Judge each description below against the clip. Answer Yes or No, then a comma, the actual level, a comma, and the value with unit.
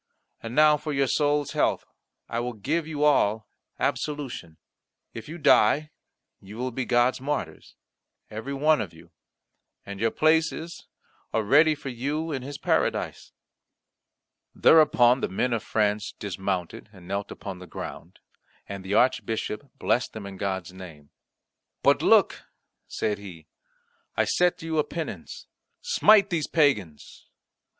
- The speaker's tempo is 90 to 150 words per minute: Yes, average, 140 wpm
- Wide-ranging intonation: Yes, wide, 6.9 semitones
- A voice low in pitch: Yes, low, 120 Hz